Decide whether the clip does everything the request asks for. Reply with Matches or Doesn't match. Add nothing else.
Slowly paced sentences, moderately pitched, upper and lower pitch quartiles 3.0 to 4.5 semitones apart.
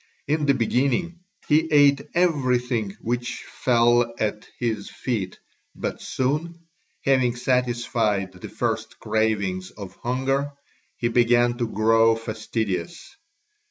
Doesn't match